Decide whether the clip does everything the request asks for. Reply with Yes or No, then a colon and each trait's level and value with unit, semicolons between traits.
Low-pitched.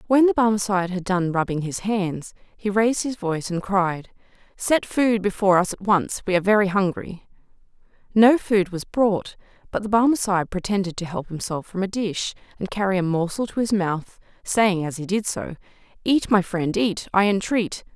No: high, 195 Hz